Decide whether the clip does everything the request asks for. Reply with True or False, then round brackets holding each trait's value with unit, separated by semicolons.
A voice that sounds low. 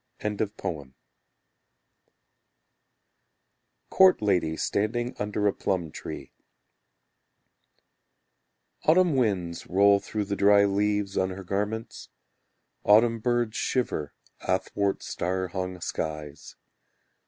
True (100 Hz)